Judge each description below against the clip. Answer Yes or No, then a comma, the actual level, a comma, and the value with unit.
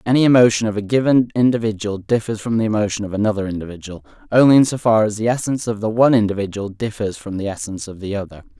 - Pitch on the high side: No, low, 110 Hz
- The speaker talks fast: Yes, fast, 215 wpm